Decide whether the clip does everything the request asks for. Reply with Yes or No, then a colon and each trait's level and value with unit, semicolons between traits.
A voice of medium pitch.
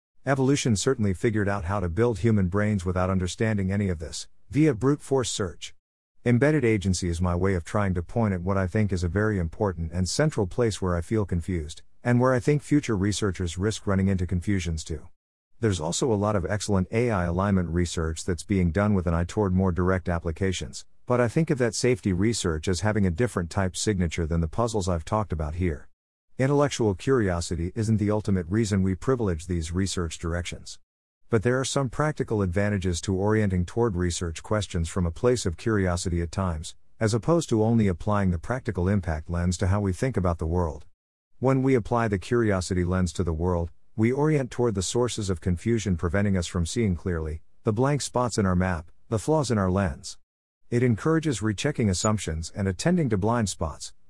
No: very low, 95 Hz